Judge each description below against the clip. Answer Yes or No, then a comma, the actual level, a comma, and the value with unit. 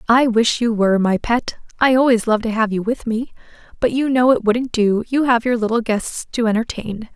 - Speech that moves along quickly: Yes, fast, 225 wpm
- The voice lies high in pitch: Yes, high, 230 Hz